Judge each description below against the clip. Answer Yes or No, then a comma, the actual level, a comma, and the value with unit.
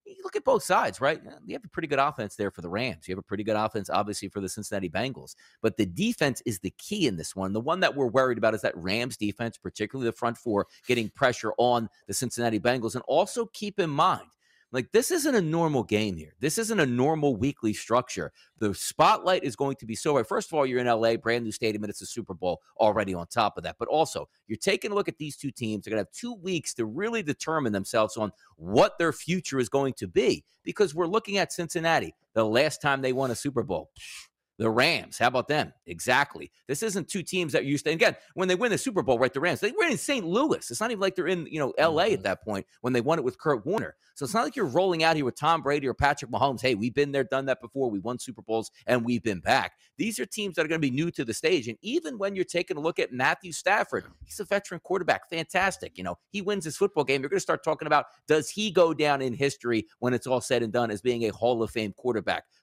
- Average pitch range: No, wide, 7.8 semitones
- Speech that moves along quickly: Yes, fast, 265 wpm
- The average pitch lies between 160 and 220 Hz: No, low, 135 Hz